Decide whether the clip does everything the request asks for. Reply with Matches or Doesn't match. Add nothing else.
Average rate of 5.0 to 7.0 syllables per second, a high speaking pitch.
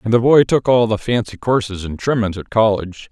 Doesn't match